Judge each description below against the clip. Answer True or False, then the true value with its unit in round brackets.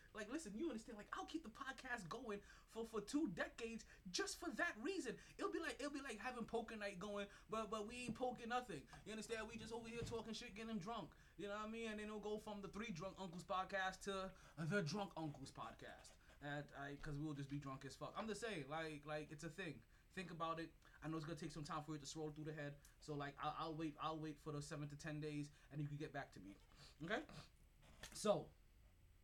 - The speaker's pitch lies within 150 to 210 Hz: True (190 Hz)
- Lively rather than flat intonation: True (6.8 semitones)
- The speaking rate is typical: False (245 wpm)